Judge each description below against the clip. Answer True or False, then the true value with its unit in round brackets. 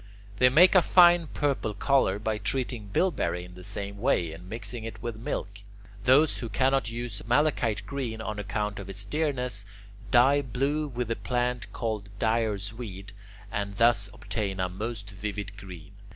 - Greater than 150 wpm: True (165 wpm)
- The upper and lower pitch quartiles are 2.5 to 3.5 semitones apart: False (3.9 semitones)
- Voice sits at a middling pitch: False (110 Hz)